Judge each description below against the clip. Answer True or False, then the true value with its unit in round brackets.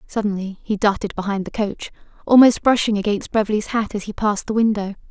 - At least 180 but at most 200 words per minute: True (190 wpm)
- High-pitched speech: True (210 Hz)